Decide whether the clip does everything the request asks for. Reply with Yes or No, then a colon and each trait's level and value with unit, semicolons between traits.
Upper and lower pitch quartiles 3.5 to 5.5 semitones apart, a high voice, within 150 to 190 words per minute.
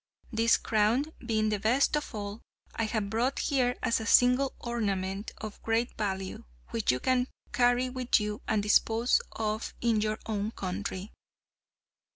No: average, 2.7 semitones; high, 220 Hz; average, 155 wpm